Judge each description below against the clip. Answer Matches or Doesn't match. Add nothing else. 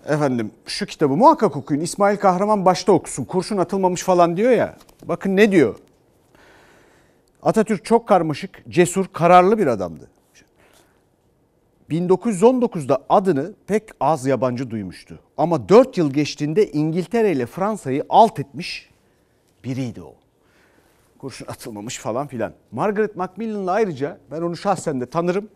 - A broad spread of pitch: Matches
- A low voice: Doesn't match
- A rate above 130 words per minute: Doesn't match